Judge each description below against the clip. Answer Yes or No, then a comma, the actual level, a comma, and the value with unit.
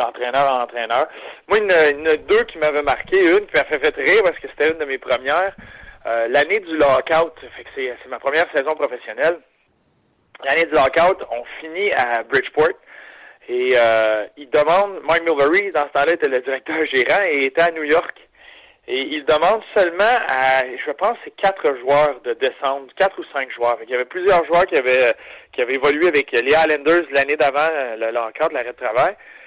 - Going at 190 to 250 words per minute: Yes, average, 200 wpm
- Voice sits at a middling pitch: Yes, medium, 170 Hz